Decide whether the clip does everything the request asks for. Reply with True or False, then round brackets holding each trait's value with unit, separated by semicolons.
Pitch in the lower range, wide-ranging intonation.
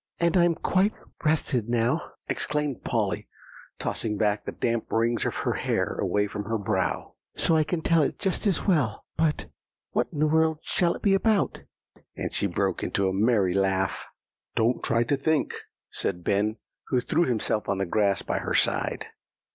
True (120 Hz; 7.5 semitones)